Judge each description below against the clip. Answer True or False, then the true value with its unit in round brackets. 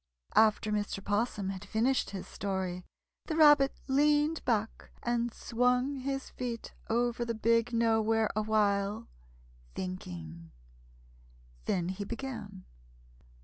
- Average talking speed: False (105 wpm)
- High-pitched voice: True (225 Hz)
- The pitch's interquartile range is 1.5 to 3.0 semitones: False (3.8 semitones)